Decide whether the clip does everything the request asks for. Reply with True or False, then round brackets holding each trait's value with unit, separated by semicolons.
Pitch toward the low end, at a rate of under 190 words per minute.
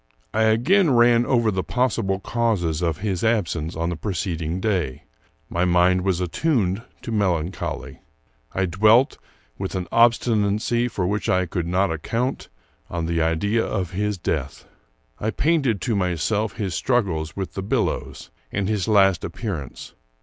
True (95 Hz; 150 wpm)